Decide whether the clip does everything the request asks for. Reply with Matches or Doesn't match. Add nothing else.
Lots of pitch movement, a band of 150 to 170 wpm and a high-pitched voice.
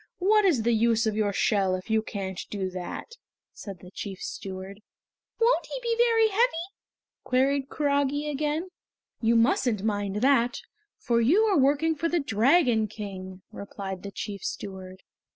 Matches